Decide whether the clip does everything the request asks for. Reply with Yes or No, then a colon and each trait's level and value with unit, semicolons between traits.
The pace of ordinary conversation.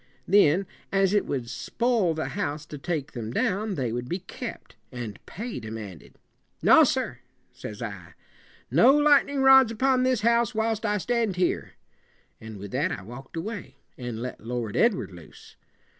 Yes: average, 175 wpm